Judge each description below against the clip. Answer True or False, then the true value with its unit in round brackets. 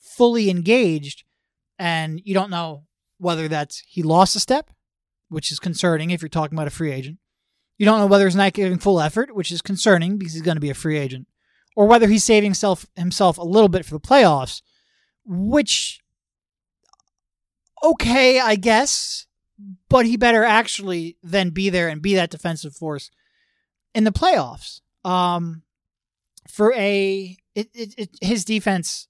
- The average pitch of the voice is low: False (190 Hz)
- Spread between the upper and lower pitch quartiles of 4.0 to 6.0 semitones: True (4.8 semitones)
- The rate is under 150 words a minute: False (165 wpm)